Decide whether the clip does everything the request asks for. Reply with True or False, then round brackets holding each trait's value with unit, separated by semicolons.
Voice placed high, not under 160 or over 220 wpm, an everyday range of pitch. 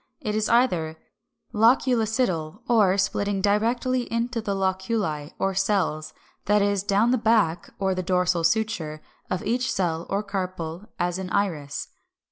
False (195 Hz; 145 wpm; 3.8 semitones)